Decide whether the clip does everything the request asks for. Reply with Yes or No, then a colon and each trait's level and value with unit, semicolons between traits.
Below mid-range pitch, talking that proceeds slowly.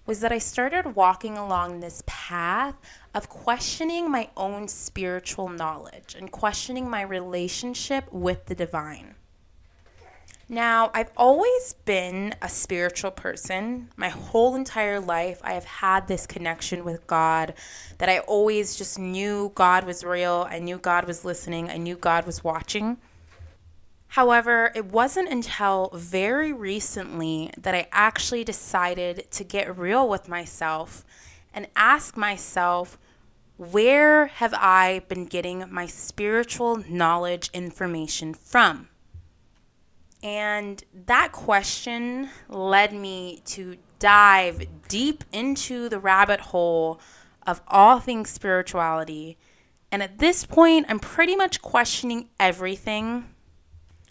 No: high, 190 Hz; slow, 120 wpm